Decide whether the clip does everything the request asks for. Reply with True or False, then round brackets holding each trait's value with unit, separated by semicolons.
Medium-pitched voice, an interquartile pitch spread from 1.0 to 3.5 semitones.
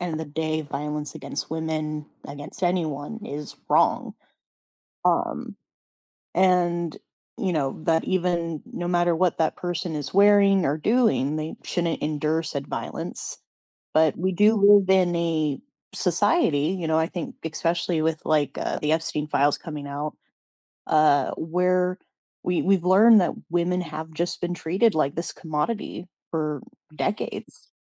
True (165 Hz; 2.9 semitones)